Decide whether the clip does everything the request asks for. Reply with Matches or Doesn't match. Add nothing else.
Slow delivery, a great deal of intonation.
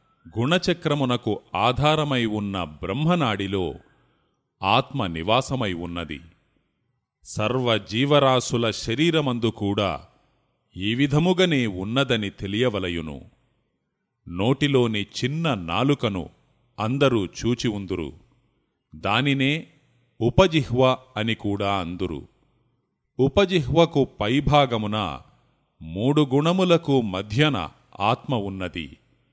Matches